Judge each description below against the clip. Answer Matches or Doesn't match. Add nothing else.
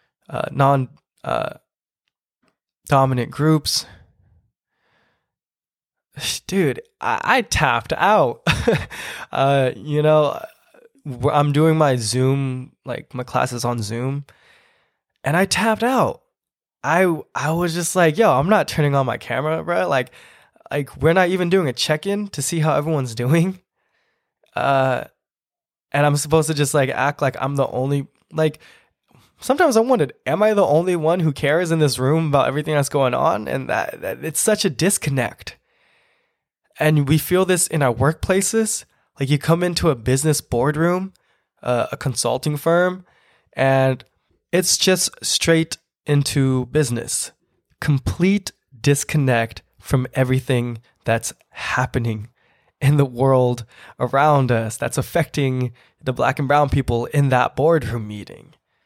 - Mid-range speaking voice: Matches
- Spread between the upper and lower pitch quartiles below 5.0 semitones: Matches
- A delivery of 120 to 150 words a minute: Matches